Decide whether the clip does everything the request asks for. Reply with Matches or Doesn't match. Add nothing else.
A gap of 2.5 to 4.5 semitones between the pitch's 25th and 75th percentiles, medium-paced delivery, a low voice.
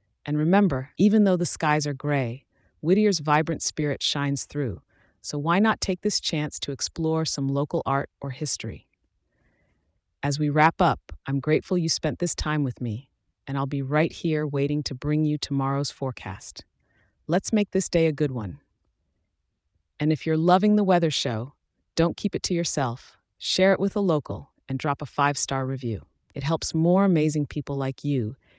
Doesn't match